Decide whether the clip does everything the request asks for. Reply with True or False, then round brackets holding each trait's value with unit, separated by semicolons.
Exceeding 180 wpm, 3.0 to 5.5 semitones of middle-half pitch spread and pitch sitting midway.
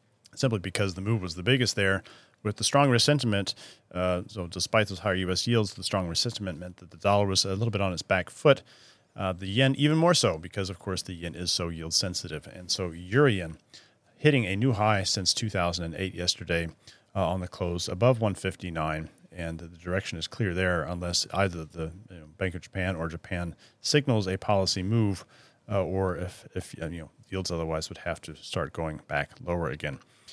False (200 wpm; 3.3 semitones; 95 Hz)